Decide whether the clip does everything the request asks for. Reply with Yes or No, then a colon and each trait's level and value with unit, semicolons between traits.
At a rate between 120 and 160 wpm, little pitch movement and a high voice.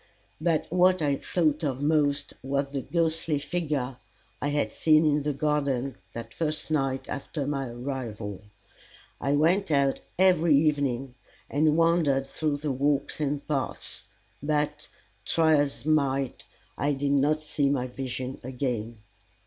No: average, 140 wpm; narrow, 2.3 semitones; medium, 145 Hz